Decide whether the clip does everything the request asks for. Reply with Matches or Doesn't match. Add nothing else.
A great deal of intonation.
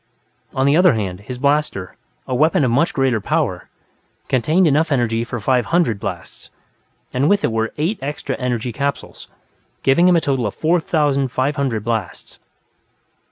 Doesn't match